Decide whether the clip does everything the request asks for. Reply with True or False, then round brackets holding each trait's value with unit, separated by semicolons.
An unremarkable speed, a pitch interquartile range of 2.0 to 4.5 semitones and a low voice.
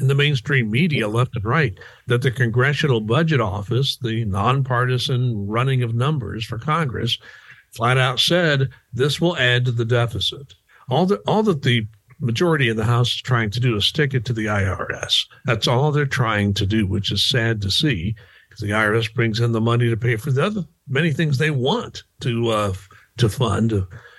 True (195 wpm; 3.4 semitones; 120 Hz)